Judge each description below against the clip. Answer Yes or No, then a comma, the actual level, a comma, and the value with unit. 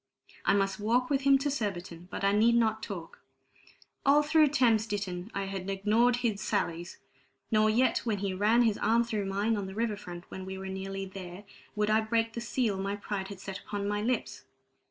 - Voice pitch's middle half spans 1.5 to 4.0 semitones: Yes, average, 3.1 semitones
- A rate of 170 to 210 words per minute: Yes, fast, 205 wpm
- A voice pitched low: No, high, 210 Hz